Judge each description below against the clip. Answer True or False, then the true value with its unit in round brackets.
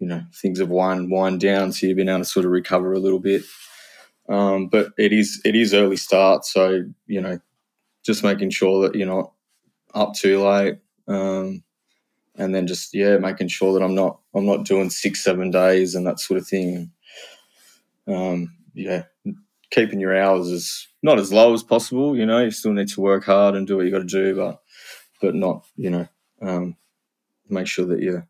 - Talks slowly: False (200 wpm)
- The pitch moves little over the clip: True (1.3 semitones)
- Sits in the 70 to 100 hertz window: True (95 Hz)